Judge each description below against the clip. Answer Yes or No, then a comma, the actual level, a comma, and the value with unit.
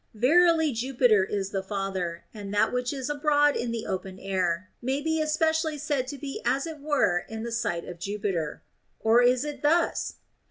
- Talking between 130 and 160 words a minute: No, average, 190 wpm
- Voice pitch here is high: Yes, high, 245 Hz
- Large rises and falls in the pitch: Yes, wide, 6.9 semitones